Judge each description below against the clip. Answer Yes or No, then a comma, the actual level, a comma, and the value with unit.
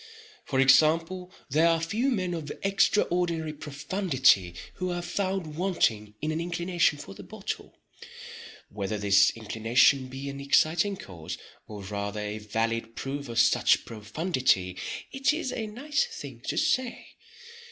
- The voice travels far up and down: Yes, wide, 8.3 semitones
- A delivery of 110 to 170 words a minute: Yes, average, 140 wpm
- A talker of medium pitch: Yes, medium, 150 Hz